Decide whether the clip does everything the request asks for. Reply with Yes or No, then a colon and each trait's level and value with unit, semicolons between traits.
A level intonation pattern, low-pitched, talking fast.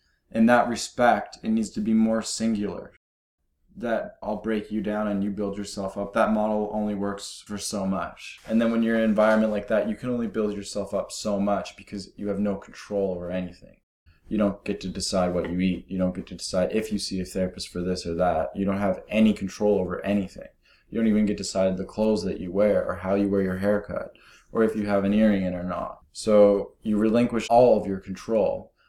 Yes: narrow, 2.2 semitones; low, 100 Hz; fast, 235 wpm